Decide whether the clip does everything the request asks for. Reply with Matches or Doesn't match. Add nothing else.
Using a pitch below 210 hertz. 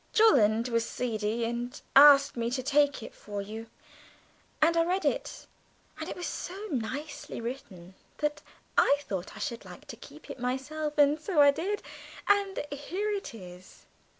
Doesn't match